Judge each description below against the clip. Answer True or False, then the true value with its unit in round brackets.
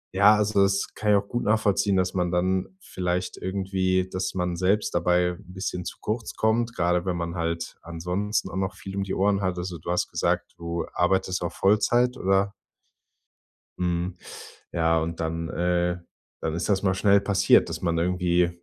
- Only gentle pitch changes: True (2.1 semitones)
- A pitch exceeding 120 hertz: False (95 Hz)